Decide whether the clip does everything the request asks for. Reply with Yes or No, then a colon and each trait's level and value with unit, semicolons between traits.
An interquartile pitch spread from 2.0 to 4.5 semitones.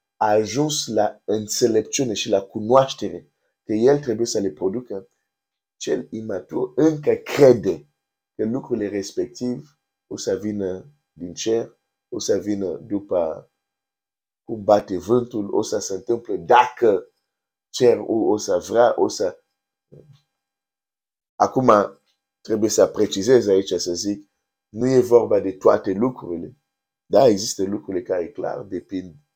No: average, 5.2 semitones